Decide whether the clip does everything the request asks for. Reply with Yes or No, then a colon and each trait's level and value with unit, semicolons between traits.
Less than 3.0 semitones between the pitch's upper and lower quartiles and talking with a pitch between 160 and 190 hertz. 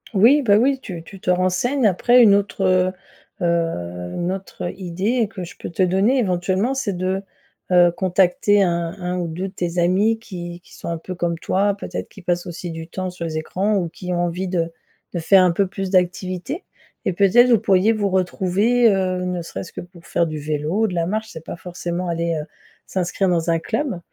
Yes: narrow, 2.5 semitones; medium, 185 Hz